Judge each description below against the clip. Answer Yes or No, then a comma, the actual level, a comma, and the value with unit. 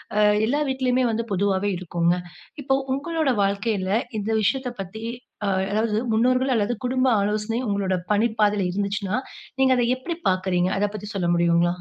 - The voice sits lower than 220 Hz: Yes, high, 210 Hz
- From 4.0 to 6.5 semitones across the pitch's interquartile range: Yes, average, 4.7 semitones